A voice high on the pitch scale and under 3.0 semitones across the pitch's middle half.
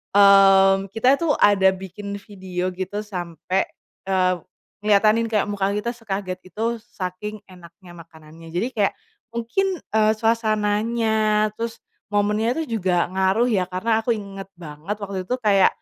Yes: high, 200 Hz; narrow, 2.5 semitones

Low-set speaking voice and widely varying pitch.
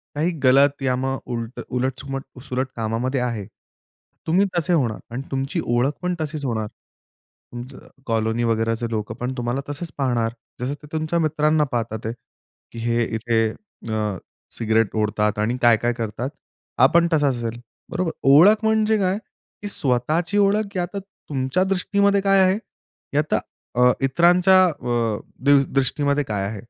Yes: low, 130 Hz; wide, 5.7 semitones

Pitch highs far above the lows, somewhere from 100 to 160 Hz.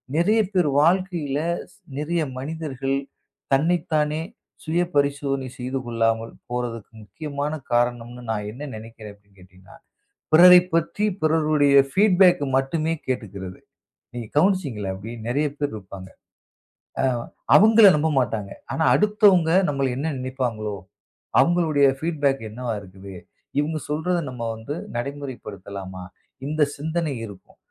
Yes: wide, 5.8 semitones; medium, 140 Hz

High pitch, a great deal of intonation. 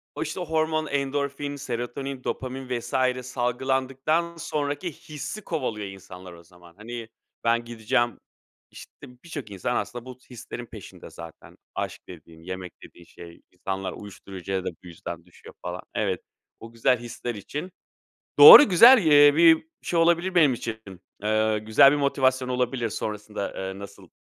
No: low, 120 Hz; wide, 6.0 semitones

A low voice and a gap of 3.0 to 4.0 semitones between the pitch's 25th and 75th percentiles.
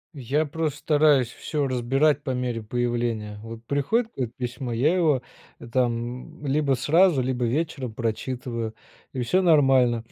Yes: low, 130 Hz; average, 3.7 semitones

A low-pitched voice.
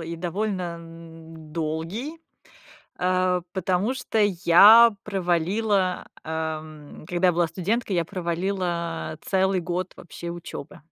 No: medium, 175 Hz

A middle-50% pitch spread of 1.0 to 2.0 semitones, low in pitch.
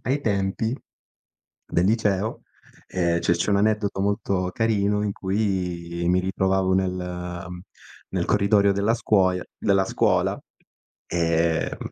No: narrow, 2.4 semitones; very low, 95 Hz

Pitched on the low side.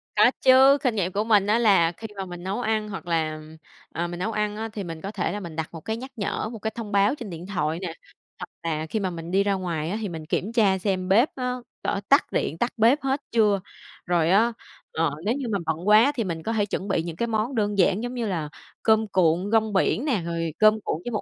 No: high, 200 Hz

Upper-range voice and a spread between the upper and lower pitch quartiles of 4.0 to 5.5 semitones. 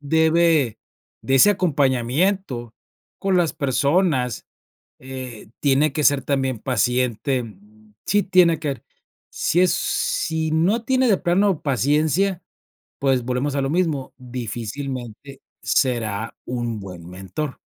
No: medium, 140 Hz; average, 4.9 semitones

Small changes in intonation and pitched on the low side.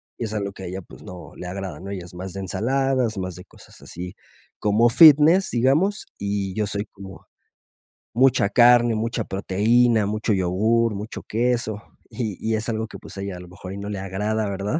No: average, 3.5 semitones; low, 105 Hz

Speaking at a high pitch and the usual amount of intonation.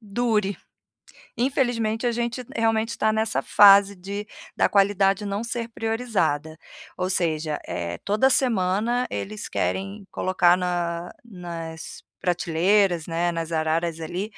Yes: high, 195 Hz; average, 4.4 semitones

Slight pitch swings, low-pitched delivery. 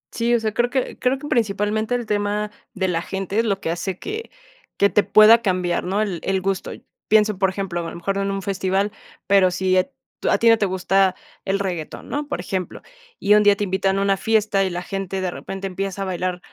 No: narrow, 2.1 semitones; high, 195 Hz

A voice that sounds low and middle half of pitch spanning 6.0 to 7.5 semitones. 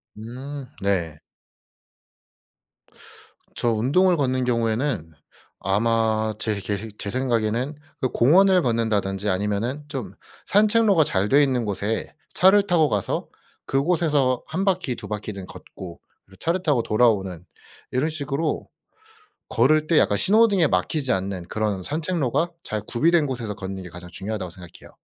Yes: low, 120 Hz; wide, 7.0 semitones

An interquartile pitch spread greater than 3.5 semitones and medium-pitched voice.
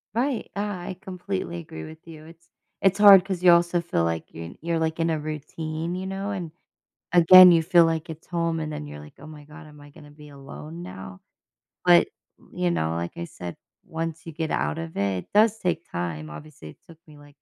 Yes: average, 4.0 semitones; medium, 160 Hz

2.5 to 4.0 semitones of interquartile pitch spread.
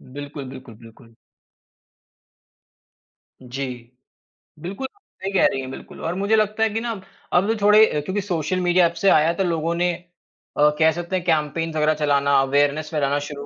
No: average, 4.7 semitones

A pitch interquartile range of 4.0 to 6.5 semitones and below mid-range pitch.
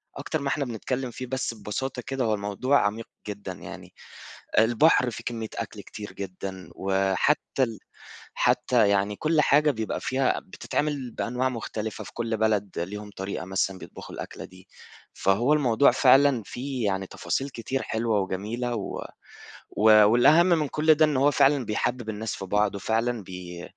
Yes: average, 4.7 semitones; low, 115 Hz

